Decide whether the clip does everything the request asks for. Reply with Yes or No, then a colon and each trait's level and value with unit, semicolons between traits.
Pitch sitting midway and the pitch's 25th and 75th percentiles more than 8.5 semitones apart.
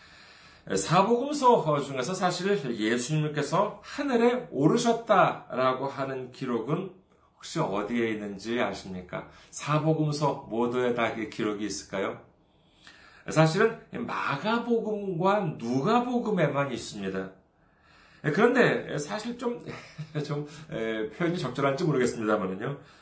Yes: medium, 150 Hz; wide, 9.0 semitones